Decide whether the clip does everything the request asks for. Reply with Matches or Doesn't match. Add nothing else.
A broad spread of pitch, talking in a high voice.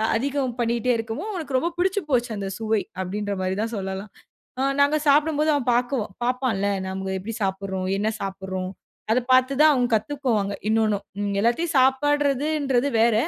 Matches